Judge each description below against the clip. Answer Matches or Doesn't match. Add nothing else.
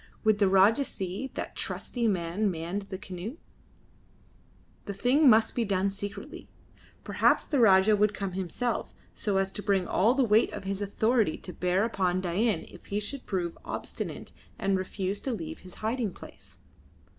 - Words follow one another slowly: Doesn't match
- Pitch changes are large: Doesn't match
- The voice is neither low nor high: Doesn't match